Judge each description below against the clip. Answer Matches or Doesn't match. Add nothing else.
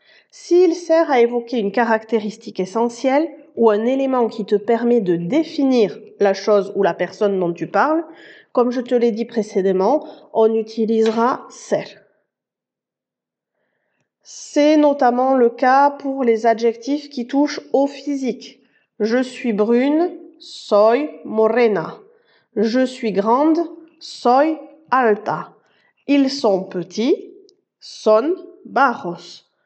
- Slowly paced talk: Matches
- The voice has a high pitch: Matches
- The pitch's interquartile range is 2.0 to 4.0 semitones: Doesn't match